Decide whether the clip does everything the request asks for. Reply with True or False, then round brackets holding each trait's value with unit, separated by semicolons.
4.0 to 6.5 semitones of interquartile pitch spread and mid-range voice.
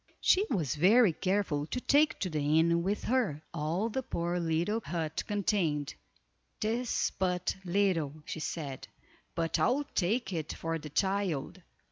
True (4.6 semitones; 175 Hz)